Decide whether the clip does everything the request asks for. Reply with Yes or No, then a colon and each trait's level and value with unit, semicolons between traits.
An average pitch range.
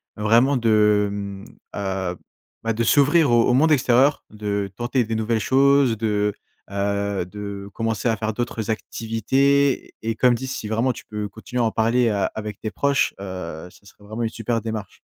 Yes: average, 3.0 semitones